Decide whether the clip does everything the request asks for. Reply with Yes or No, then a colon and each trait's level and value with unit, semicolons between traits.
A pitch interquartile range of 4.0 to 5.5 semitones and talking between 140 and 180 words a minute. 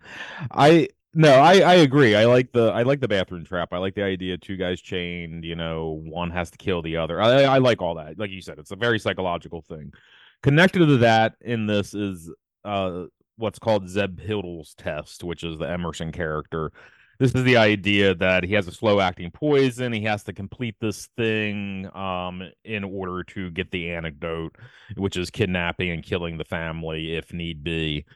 No: average, 4.3 semitones; average, 200 wpm